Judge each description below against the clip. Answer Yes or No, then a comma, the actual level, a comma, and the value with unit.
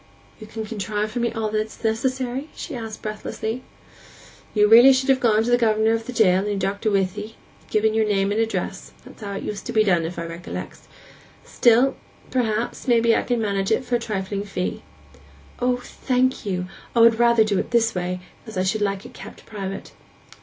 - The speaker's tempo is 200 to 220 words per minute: Yes, fast, 205 wpm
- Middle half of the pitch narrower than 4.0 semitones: Yes, average, 2.9 semitones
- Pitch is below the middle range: No, high, 220 Hz